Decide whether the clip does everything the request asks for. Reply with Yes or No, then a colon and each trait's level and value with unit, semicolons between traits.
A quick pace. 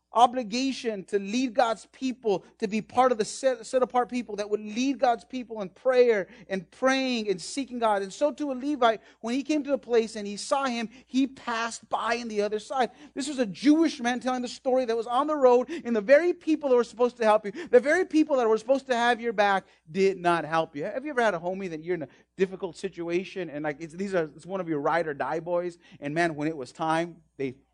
Yes: fast, 250 wpm